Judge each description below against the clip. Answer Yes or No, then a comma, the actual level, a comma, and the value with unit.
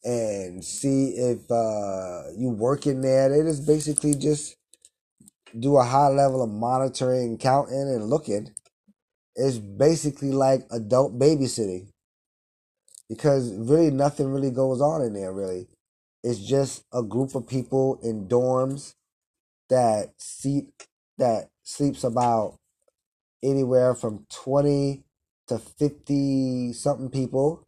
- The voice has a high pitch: No, low, 130 Hz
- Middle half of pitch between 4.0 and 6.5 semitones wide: No, average, 3.0 semitones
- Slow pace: Yes, slow, 120 wpm